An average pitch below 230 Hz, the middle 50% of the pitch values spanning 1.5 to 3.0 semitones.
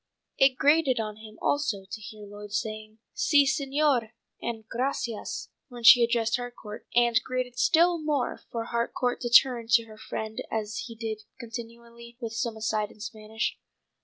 No: high, 235 Hz; narrow, 2.6 semitones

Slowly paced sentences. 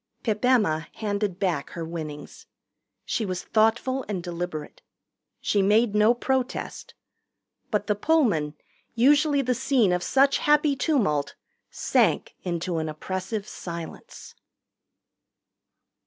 Yes: slow, 110 wpm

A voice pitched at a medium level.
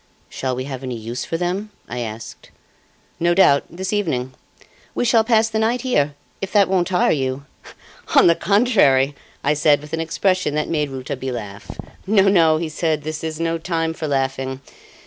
Yes: medium, 155 Hz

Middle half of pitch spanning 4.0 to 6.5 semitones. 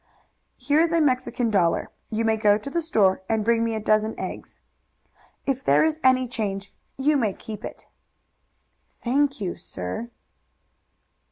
Yes: average, 4.3 semitones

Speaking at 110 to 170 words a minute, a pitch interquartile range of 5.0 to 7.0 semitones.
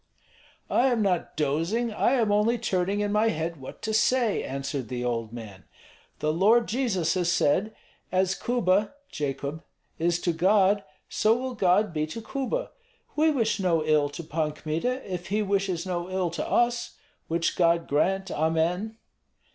Yes: average, 165 wpm; average, 5.3 semitones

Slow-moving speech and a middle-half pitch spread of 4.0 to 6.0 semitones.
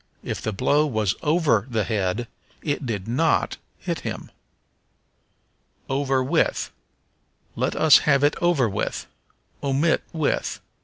Yes: slow, 120 wpm; average, 5.2 semitones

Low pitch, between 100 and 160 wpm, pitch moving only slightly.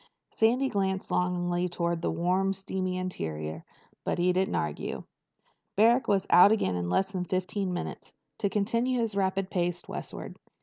No: medium, 185 Hz; average, 155 wpm; narrow, 2.1 semitones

